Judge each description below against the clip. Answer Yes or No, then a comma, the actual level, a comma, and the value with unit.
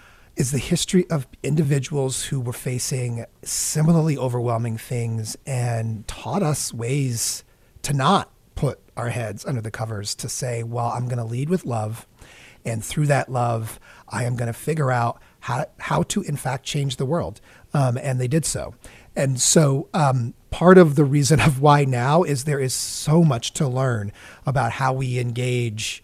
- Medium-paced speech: Yes, average, 175 wpm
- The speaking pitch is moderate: No, low, 130 Hz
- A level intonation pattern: No, average, 3.8 semitones